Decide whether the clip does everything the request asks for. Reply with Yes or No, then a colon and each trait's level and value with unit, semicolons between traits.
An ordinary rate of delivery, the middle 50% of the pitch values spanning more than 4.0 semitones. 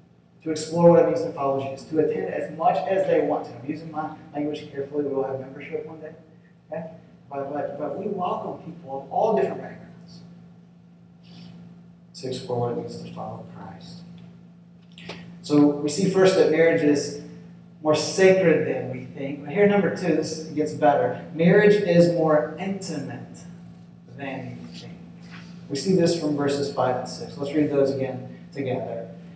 No: average, 175 wpm; average, 3.1 semitones